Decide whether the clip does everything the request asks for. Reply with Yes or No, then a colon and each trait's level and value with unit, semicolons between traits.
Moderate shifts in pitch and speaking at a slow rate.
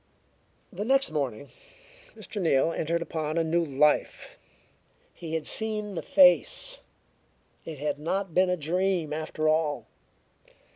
Yes: average, 3.9 semitones; slow, 130 wpm